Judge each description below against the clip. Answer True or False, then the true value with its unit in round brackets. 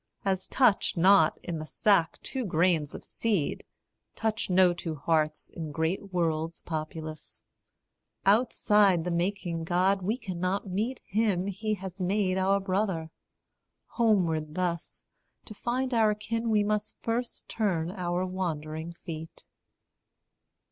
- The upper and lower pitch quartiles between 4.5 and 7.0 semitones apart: False (4.0 semitones)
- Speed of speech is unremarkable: False (125 wpm)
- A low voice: False (185 Hz)